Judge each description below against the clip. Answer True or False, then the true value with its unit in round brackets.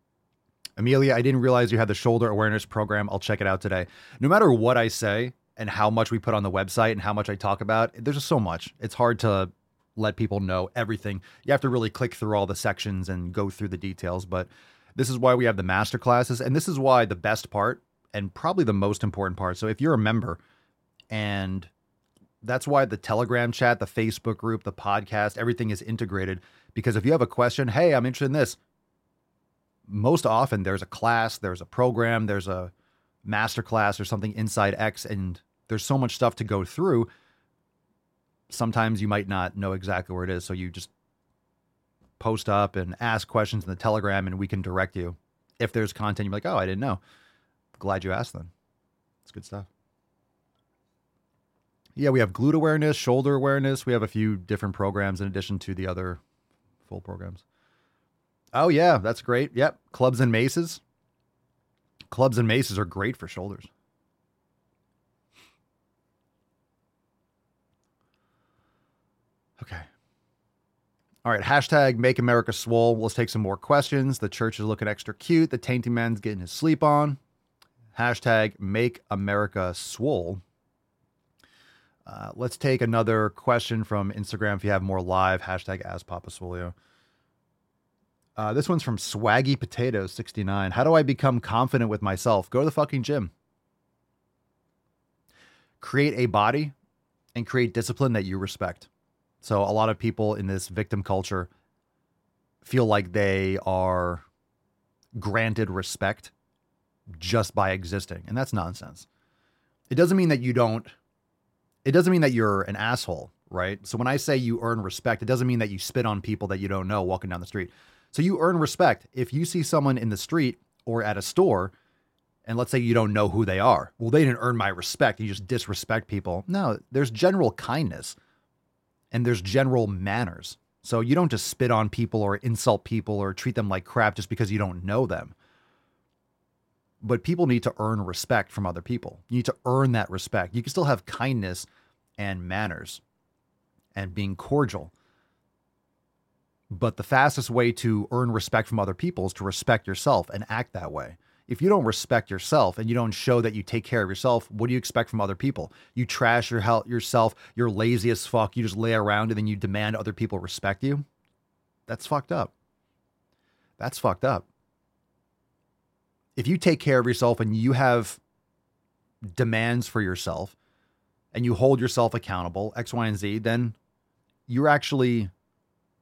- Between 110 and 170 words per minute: False (180 wpm)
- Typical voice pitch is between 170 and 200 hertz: False (110 Hz)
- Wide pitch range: False (3.8 semitones)